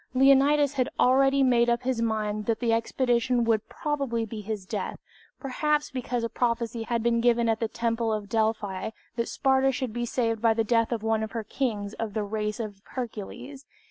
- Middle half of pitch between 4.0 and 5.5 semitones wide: No, narrow, 2.5 semitones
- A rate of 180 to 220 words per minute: Yes, average, 195 wpm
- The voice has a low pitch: No, high, 230 Hz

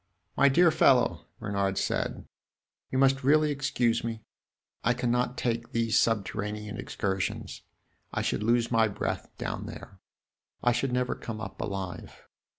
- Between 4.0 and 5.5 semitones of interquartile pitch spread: No, average, 3.3 semitones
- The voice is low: Yes, low, 115 Hz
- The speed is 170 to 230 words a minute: No, average, 140 wpm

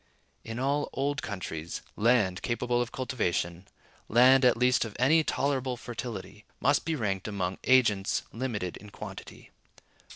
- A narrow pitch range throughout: No, average, 4.3 semitones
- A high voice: No, low, 120 Hz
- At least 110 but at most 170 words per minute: Yes, slow, 135 wpm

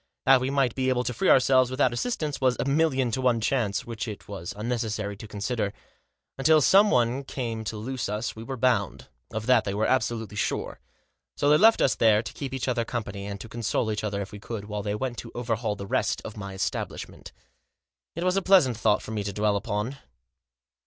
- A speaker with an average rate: No, fast, 220 wpm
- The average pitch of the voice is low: Yes, low, 115 Hz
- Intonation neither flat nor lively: Yes, average, 3.8 semitones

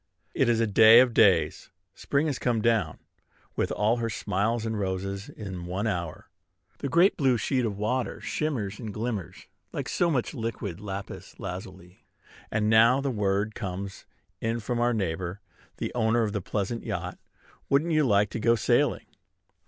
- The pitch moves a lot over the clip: No, average, 3.3 semitones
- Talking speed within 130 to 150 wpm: No, average, 170 wpm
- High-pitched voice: No, low, 110 Hz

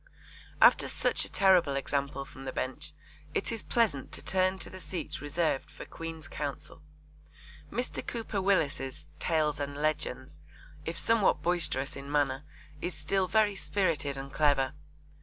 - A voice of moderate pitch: Yes, medium, 155 Hz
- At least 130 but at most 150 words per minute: Yes, average, 145 wpm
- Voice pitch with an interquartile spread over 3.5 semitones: Yes, average, 5.0 semitones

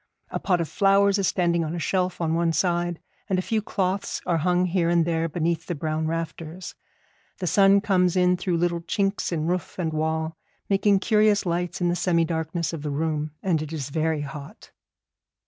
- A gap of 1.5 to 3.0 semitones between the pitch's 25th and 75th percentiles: Yes, narrow, 2.4 semitones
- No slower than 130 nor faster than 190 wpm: No, average, 200 wpm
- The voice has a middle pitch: Yes, medium, 170 Hz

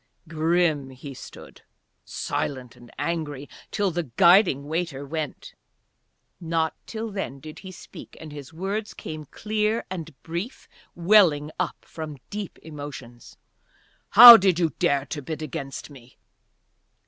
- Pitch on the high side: No, medium, 160 Hz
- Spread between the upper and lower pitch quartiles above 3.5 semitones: Yes, average, 4.3 semitones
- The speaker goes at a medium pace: No, slow, 130 wpm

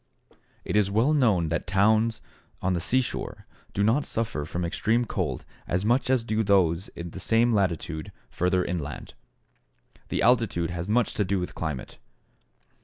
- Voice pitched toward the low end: Yes, low, 100 Hz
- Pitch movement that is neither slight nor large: Yes, average, 4.8 semitones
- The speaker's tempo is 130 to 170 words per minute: Yes, average, 160 wpm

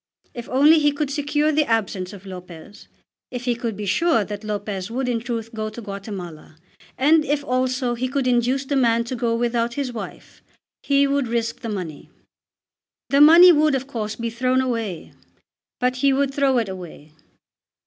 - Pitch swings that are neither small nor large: Yes, average, 4.4 semitones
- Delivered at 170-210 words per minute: Yes, average, 180 wpm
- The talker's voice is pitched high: Yes, high, 240 Hz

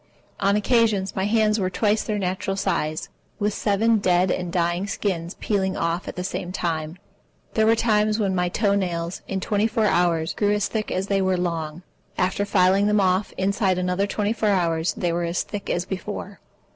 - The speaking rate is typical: Yes, average, 195 wpm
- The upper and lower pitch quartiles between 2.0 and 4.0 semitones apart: Yes, average, 2.7 semitones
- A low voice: No, high, 190 Hz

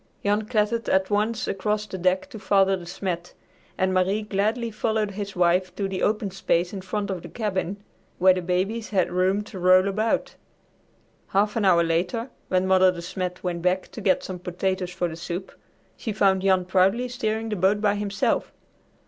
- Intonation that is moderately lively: No, narrow, 2.3 semitones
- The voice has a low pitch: No, high, 190 Hz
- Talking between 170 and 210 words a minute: Yes, average, 190 wpm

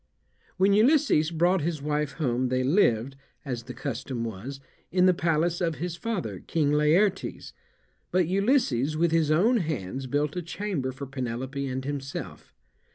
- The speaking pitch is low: No, medium, 150 Hz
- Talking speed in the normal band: Yes, average, 155 wpm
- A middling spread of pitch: Yes, average, 5.0 semitones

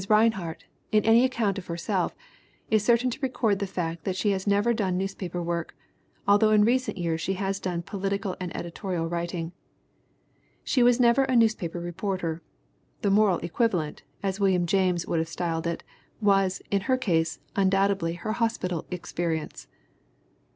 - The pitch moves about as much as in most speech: Yes, average, 3.8 semitones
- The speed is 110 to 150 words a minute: No, average, 160 wpm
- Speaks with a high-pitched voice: Yes, high, 195 Hz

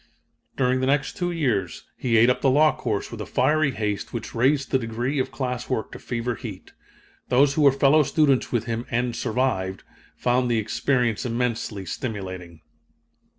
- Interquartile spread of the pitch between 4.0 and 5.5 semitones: No, average, 3.3 semitones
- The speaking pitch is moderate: No, low, 125 Hz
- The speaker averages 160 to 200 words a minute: Yes, average, 175 wpm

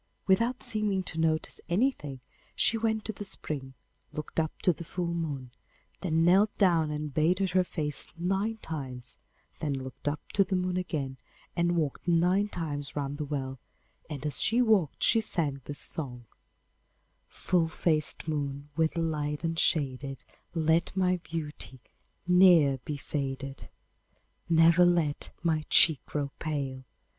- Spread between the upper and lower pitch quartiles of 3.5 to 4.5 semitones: Yes, average, 4.0 semitones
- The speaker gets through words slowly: No, average, 145 wpm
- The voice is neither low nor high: Yes, medium, 160 Hz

